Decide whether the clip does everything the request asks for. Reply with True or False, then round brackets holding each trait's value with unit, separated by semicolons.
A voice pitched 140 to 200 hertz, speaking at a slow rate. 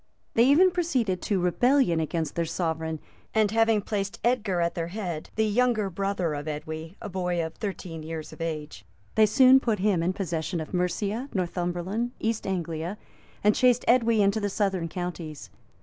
False (190 Hz; 170 wpm)